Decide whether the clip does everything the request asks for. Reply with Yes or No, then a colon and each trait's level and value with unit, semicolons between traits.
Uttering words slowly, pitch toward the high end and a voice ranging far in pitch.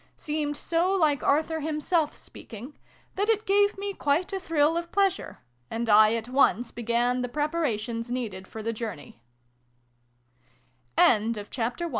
Yes: slow, 125 wpm; very high, 290 Hz; wide, 6.4 semitones